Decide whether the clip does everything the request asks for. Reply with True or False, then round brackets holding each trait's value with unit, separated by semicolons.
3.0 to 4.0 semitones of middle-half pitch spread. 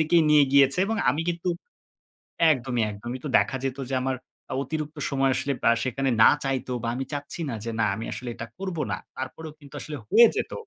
True (3.3 semitones)